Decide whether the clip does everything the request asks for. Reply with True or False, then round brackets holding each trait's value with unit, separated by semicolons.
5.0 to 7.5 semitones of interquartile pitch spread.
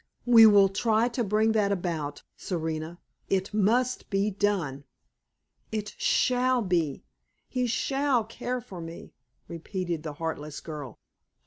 True (5.6 semitones)